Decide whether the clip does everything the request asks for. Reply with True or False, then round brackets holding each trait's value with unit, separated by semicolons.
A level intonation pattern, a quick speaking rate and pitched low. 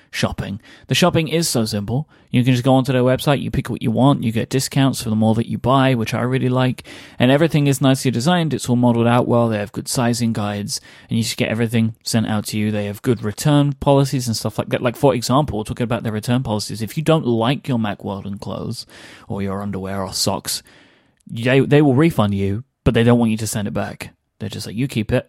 False (3.5 semitones; 250 wpm; 120 Hz)